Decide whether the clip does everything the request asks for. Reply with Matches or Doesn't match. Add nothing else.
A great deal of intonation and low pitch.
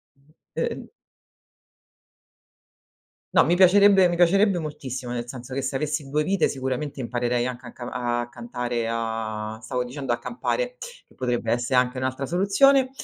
Matches